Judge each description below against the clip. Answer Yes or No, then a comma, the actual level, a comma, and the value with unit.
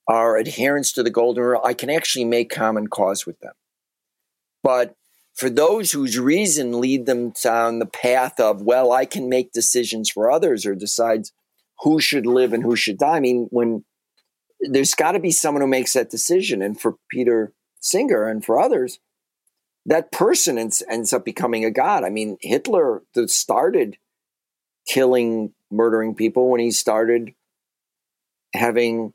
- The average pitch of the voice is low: Yes, low, 120 Hz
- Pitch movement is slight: Yes, narrow, 2.2 semitones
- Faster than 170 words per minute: No, average, 165 wpm